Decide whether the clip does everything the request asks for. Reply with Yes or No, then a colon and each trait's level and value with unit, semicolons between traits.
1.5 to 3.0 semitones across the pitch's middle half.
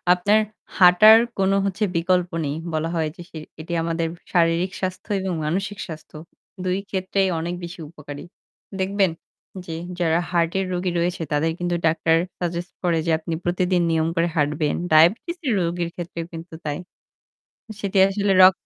Yes: narrow, 2.4 semitones